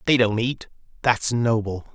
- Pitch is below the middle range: Yes, low, 115 Hz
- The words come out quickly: No, average, 155 wpm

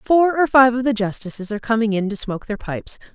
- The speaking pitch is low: No, high, 230 Hz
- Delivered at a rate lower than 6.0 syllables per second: No, 6.6 syllables/s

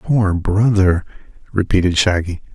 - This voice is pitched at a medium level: No, very low, 95 Hz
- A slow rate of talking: Yes, slow, 95 wpm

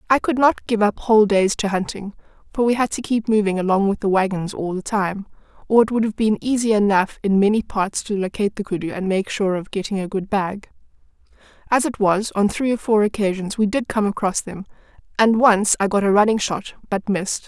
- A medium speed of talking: No, fast, 220 wpm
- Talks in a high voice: Yes, high, 205 Hz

